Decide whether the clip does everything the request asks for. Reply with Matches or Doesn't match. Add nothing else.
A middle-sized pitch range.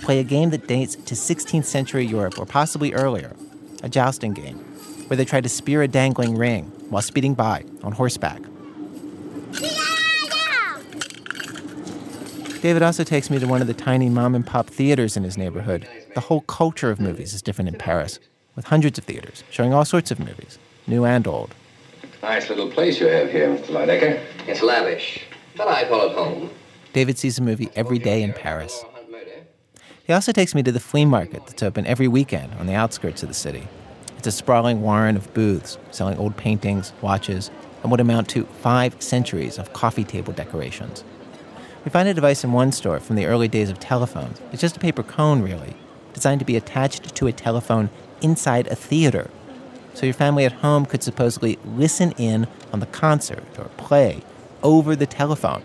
Matches